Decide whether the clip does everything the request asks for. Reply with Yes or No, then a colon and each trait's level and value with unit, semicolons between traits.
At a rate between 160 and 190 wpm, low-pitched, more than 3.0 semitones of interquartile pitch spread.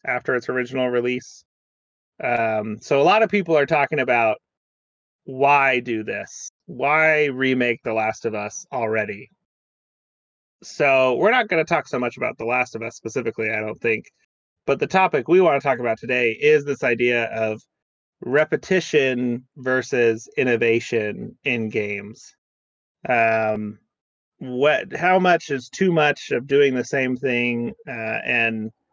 No: average, 150 wpm; low, 120 Hz; average, 3.9 semitones